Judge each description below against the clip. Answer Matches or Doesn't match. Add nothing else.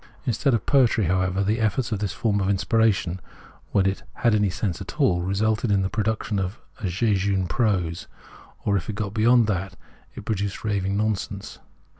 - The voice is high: Doesn't match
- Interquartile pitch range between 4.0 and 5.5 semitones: Doesn't match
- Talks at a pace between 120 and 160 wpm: Doesn't match